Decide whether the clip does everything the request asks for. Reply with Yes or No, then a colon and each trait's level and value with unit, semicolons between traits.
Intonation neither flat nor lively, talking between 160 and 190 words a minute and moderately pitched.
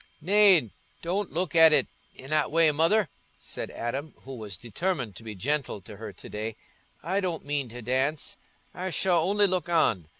No: wide, 6.9 semitones; average, 175 wpm; medium, 150 Hz